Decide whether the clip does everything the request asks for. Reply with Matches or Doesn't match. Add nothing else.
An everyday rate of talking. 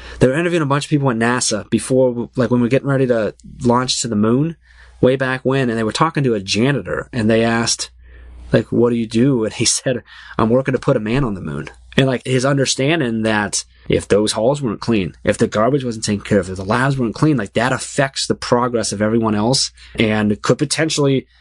Doesn't match